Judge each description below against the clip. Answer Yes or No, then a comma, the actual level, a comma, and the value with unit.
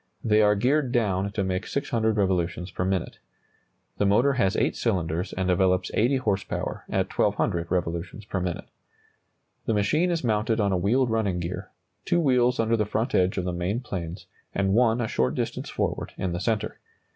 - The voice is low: Yes, low, 100 Hz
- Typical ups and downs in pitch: Yes, average, 3.9 semitones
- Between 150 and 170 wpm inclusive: No, average, 185 wpm